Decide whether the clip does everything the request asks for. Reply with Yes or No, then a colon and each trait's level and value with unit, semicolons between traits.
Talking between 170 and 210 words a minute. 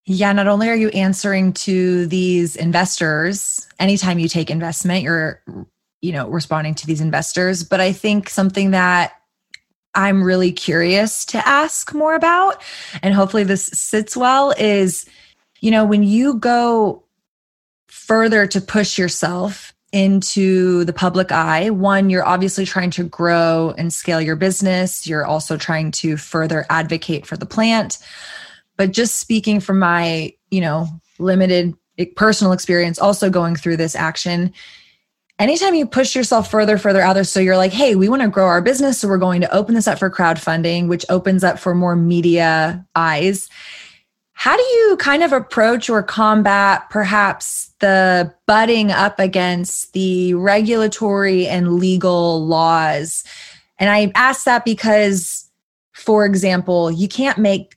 No: average, 155 wpm